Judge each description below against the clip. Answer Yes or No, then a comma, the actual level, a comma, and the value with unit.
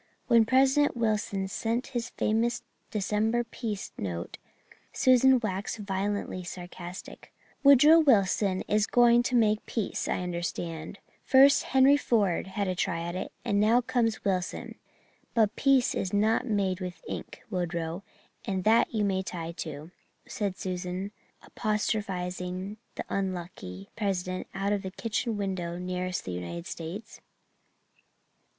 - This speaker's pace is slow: Yes, slow, 130 wpm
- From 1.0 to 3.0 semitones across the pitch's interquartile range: No, average, 4.0 semitones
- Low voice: No, high, 200 Hz